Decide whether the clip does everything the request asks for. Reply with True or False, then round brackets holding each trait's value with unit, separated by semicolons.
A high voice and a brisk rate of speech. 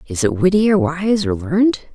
True (215 Hz; 215 wpm)